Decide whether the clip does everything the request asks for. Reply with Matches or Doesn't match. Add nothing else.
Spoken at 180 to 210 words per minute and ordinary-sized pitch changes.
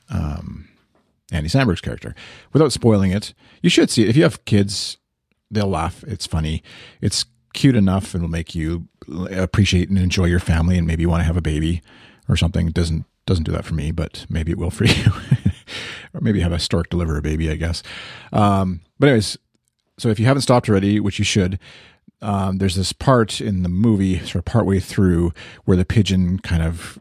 Matches